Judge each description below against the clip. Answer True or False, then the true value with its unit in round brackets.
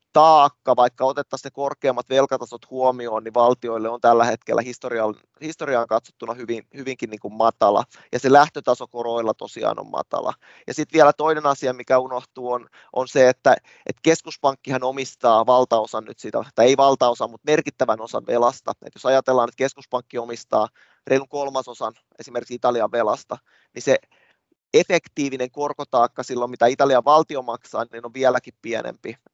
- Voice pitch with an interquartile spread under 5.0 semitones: True (2.7 semitones)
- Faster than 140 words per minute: True (150 wpm)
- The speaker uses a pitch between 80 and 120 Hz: False (130 Hz)